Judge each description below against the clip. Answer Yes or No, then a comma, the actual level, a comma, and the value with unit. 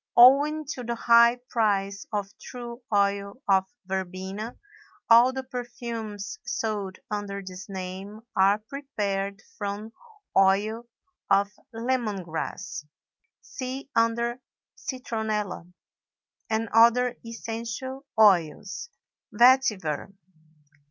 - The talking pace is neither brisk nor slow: No, slow, 90 wpm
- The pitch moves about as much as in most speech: Yes, average, 3.3 semitones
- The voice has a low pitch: No, high, 220 Hz